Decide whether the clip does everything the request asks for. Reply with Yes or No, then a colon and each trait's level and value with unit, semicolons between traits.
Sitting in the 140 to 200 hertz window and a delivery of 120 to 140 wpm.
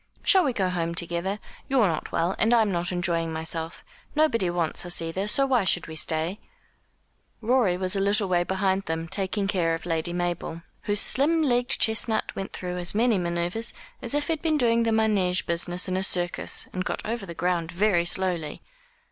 No: medium, 185 Hz; average, 195 wpm